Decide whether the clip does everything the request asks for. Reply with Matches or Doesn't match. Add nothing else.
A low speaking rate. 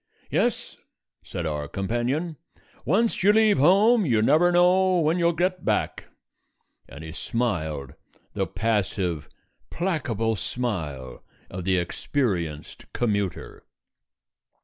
Matches